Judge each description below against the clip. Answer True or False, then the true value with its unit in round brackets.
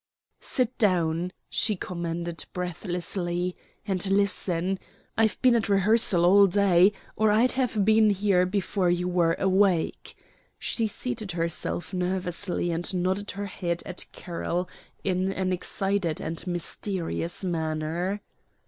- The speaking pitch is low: False (185 Hz)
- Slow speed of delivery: True (120 wpm)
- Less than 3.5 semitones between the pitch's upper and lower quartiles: True (2.6 semitones)